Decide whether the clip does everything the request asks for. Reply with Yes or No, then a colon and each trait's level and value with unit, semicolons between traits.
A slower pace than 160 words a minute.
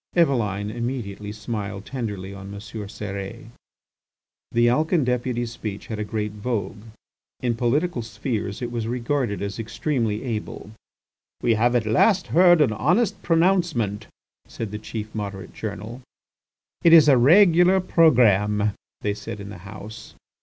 Yes: average, 140 wpm